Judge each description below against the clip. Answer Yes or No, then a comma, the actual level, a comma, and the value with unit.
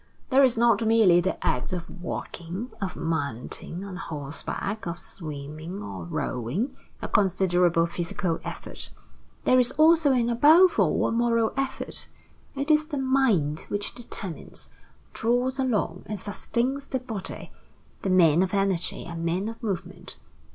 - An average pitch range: No, wide, 6.5 semitones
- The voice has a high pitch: Yes, high, 200 Hz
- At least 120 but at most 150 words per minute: Yes, average, 145 wpm